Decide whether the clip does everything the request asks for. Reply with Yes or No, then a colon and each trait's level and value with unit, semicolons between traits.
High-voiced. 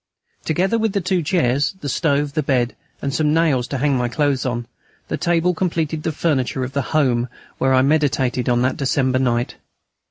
No: medium, 140 Hz